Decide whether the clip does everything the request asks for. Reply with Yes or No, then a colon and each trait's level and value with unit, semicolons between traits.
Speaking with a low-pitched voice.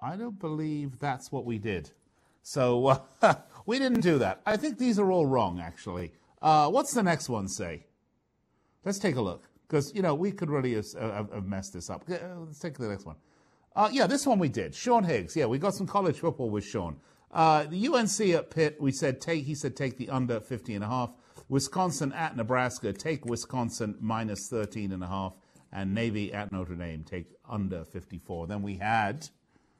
Yes: low, 130 Hz